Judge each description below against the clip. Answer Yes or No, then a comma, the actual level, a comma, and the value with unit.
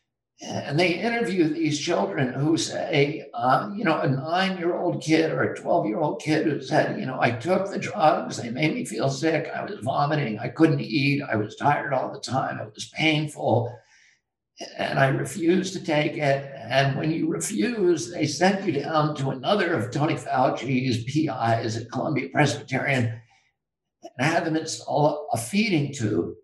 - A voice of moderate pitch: Yes, medium, 155 Hz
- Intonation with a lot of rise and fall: No, average, 3.7 semitones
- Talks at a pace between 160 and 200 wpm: Yes, average, 180 wpm